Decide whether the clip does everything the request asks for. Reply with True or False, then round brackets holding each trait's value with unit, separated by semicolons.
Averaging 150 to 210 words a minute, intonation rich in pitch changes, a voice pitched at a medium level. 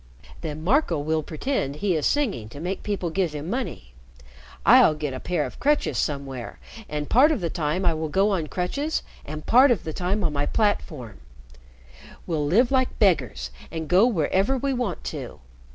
True (185 wpm; 6.5 semitones; 170 Hz)